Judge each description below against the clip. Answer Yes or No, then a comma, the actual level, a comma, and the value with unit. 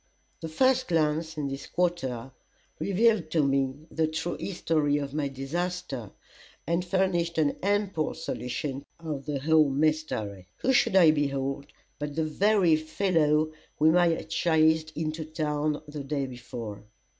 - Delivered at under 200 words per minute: Yes, average, 145 wpm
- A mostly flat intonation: No, average, 3.1 semitones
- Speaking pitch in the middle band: Yes, medium, 155 Hz